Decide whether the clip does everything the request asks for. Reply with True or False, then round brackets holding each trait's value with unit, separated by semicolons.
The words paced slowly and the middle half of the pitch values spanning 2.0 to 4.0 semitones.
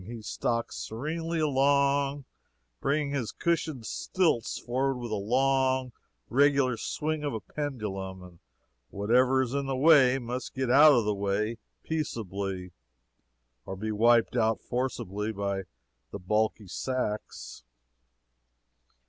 False (125 wpm; 4.6 semitones)